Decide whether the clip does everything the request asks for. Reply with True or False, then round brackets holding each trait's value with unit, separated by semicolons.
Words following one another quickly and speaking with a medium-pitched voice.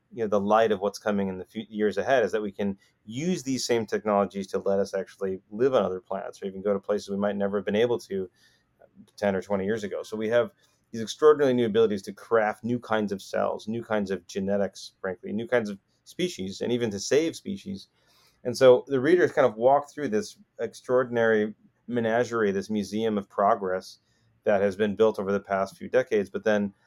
False (220 wpm; 110 Hz)